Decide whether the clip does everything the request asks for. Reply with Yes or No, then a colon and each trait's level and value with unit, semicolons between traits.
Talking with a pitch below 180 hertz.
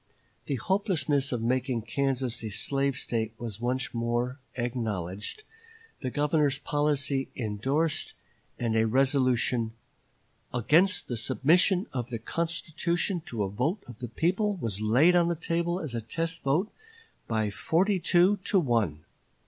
Yes: low, 135 Hz